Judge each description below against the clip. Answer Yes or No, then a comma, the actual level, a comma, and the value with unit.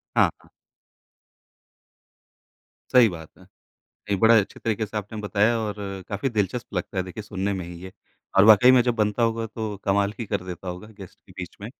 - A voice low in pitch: Yes, low, 105 Hz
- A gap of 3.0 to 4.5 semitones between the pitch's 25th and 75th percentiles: No, narrow, 2.6 semitones